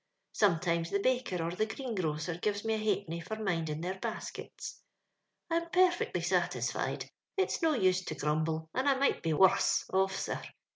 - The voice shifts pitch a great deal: Yes, wide, 6.0 semitones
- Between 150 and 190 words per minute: Yes, average, 165 wpm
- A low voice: No, high, 190 Hz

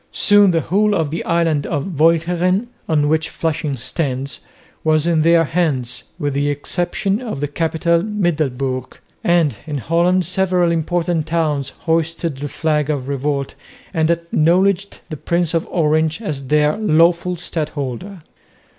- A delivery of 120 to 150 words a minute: Yes, average, 140 wpm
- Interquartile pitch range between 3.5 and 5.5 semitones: No, average, 3.0 semitones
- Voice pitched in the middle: Yes, medium, 160 Hz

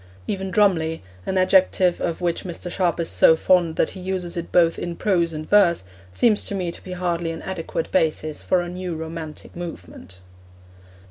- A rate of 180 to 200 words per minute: Yes, average, 185 wpm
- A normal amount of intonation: No, narrow, 2.1 semitones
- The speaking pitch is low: No, medium, 175 Hz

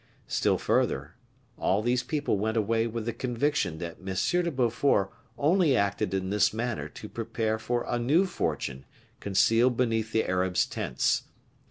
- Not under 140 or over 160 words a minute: Yes, average, 155 wpm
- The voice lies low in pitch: Yes, low, 115 Hz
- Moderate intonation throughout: Yes, average, 3.8 semitones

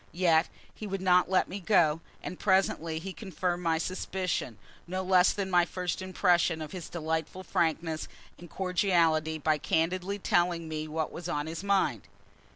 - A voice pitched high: No, medium, 175 Hz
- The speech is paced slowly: No, average, 160 wpm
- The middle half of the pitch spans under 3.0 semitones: Yes, narrow, 2.6 semitones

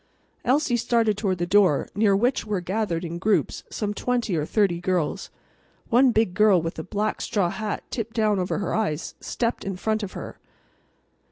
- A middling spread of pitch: Yes, average, 3.6 semitones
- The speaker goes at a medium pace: Yes, average, 180 wpm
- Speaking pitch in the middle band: No, high, 205 Hz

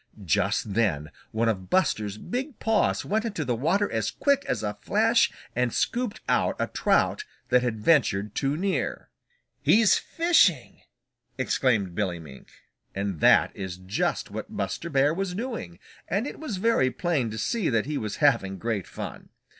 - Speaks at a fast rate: No, average, 160 wpm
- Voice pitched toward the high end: No, low, 125 Hz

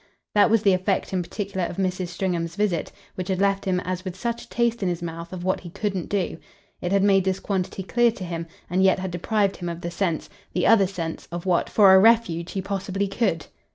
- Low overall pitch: No, high, 190 Hz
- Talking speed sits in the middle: No, fast, 235 wpm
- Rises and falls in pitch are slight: Yes, narrow, 2.1 semitones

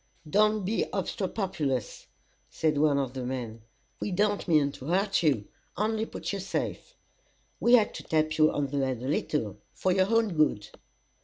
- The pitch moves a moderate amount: No, wide, 6.8 semitones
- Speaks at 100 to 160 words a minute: No, average, 170 wpm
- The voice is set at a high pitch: No, medium, 155 Hz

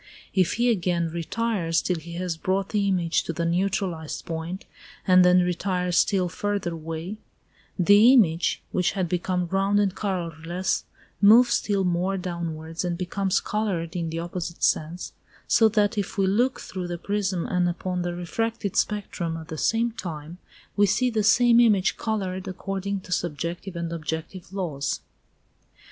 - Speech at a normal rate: Yes, average, 155 wpm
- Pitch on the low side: No, medium, 180 Hz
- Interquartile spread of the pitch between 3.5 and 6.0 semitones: No, average, 2.9 semitones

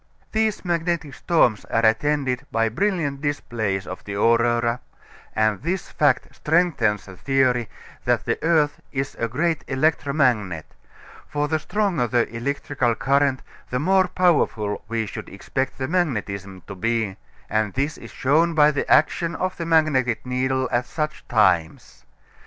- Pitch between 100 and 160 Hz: Yes, low, 135 Hz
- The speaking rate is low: No, average, 145 wpm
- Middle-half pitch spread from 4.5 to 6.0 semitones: Yes, wide, 5.5 semitones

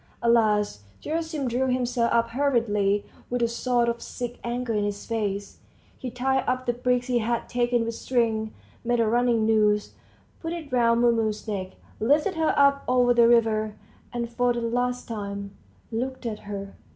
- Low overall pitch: No, high, 235 Hz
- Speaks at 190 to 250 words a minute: No, average, 175 wpm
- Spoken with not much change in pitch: Yes, narrow, 2.3 semitones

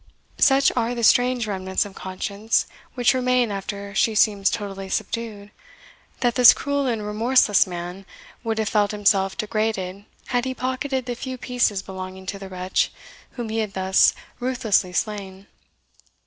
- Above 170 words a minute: No, average, 150 wpm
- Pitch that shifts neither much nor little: Yes, average, 4.0 semitones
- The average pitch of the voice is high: Yes, high, 215 Hz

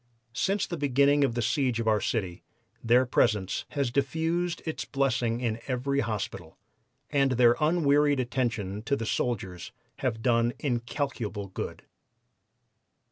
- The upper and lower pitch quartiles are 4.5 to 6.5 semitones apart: No, average, 3.7 semitones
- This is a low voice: Yes, low, 125 Hz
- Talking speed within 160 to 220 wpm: No, slow, 135 wpm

